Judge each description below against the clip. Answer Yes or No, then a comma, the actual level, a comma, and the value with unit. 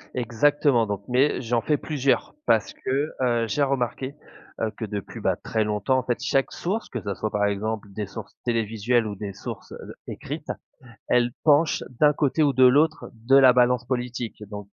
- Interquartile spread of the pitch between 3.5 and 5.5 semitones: Yes, average, 3.9 semitones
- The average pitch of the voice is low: Yes, low, 120 Hz